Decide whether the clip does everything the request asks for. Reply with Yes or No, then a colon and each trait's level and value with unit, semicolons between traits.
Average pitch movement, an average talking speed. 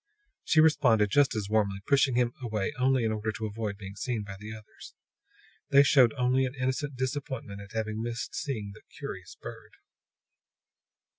Yes: average, 3.7 semitones; average, 165 wpm